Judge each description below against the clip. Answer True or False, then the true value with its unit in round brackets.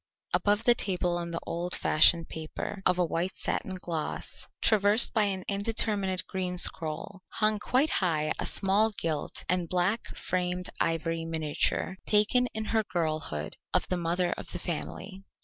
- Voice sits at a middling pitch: True (180 Hz)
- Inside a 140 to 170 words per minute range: True (155 wpm)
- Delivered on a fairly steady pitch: False (3.7 semitones)